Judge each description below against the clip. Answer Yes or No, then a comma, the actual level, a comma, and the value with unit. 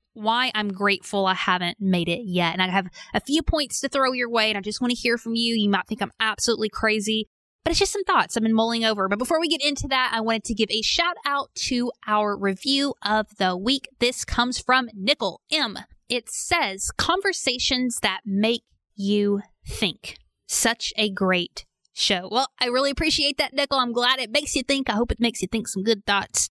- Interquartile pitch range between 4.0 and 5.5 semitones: Yes, average, 4.3 semitones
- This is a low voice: No, high, 230 Hz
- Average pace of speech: No, fast, 220 wpm